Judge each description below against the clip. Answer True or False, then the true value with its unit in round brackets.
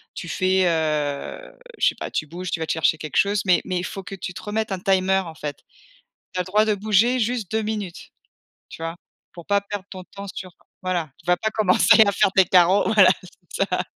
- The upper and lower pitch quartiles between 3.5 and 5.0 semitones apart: False (2.8 semitones)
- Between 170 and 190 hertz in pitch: True (185 Hz)